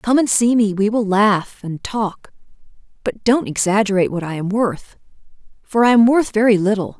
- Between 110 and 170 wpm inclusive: No, average, 190 wpm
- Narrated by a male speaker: No, female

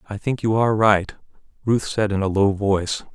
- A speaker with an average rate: No, fast, 210 wpm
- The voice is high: No, low, 105 Hz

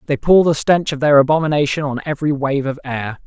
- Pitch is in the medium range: Yes, medium, 145 Hz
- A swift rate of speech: Yes, fast, 220 wpm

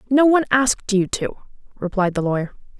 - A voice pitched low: No, high, 220 Hz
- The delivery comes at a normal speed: Yes, average, 170 wpm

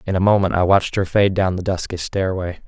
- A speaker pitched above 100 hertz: No, very low, 95 Hz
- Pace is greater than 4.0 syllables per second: Yes, 6.0 syllables/s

